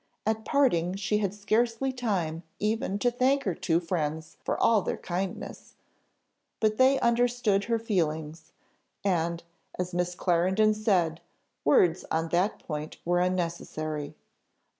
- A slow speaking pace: Yes, slow, 130 wpm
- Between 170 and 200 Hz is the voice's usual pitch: Yes, medium, 185 Hz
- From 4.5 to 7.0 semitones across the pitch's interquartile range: Yes, average, 4.8 semitones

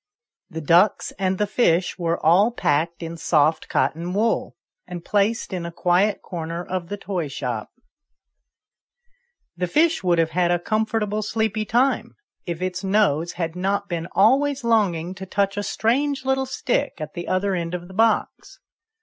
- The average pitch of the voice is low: No, medium, 185 Hz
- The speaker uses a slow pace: No, average, 165 wpm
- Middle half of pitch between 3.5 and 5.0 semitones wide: Yes, average, 4.1 semitones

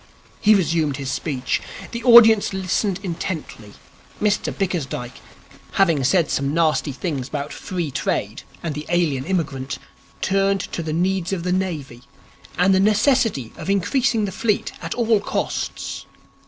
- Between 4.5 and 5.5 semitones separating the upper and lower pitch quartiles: Yes, average, 5.1 semitones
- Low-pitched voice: No, medium, 180 Hz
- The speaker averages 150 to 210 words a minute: No, average, 140 wpm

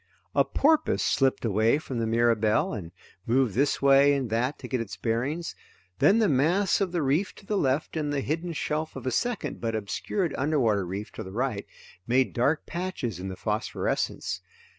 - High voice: No, low, 135 Hz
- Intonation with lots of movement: Yes, wide, 5.9 semitones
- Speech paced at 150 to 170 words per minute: No, average, 185 wpm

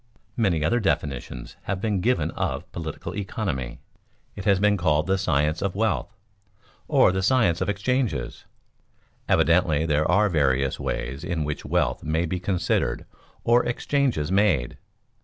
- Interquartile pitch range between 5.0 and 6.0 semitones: Yes, wide, 5.4 semitones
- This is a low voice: Yes, very low, 90 Hz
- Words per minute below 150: Yes, average, 140 wpm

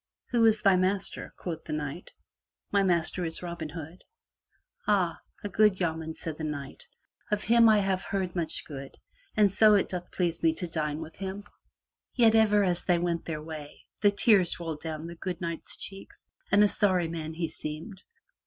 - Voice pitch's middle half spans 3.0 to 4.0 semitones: Yes, average, 3.7 semitones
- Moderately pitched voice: Yes, medium, 175 Hz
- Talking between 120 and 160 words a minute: No, average, 190 wpm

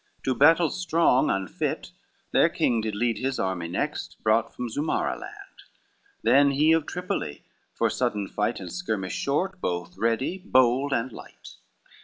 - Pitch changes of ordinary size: No, wide, 6.0 semitones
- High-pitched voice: No, low, 125 Hz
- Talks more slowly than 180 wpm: Yes, average, 150 wpm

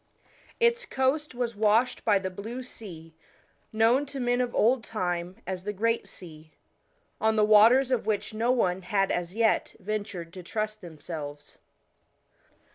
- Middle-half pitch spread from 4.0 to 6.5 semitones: Yes, average, 4.7 semitones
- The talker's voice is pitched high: Yes, high, 215 Hz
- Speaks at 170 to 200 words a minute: No, average, 155 wpm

